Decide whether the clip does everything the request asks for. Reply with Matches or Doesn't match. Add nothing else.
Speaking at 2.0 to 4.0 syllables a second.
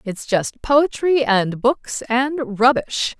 Matches